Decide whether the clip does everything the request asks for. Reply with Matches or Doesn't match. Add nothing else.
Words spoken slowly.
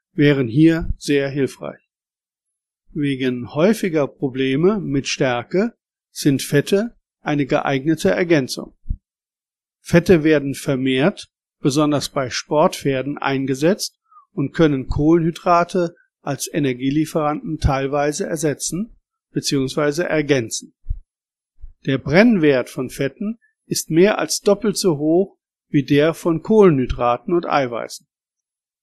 Matches